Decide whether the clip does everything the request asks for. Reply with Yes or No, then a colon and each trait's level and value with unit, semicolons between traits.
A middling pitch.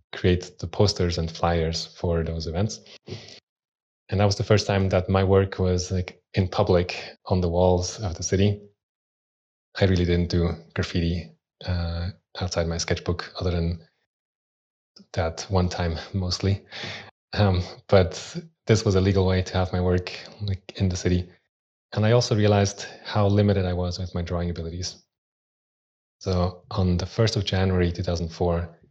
No: very low, 90 Hz